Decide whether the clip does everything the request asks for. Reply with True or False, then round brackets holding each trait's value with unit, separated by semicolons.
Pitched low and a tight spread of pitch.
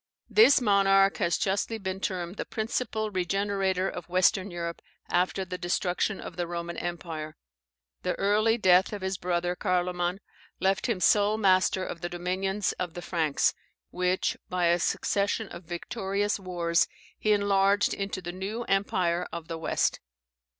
False (185 Hz; 2.3 semitones)